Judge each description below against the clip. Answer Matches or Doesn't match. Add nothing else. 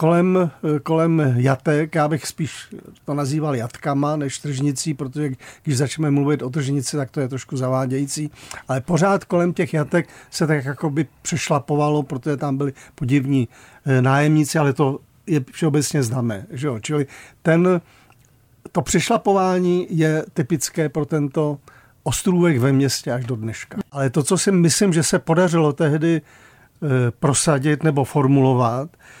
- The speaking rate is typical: Matches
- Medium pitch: Matches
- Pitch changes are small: Doesn't match